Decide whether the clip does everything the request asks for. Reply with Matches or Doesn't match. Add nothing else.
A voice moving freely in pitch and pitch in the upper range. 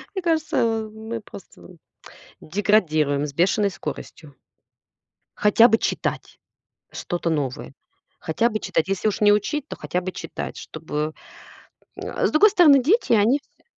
Matches